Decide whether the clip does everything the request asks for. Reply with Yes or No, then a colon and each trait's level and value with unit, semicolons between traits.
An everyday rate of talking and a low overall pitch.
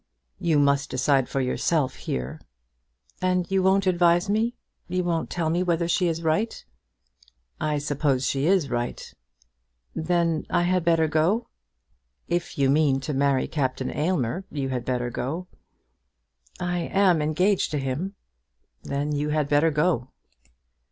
No: average, 145 wpm; medium, 155 Hz